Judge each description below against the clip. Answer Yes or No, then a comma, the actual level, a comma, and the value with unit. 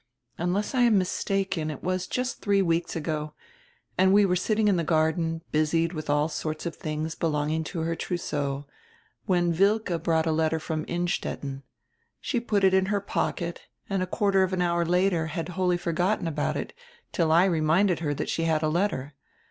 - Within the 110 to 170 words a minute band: No, average, 190 wpm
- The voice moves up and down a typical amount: Yes, average, 3.0 semitones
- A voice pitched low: No, medium, 170 Hz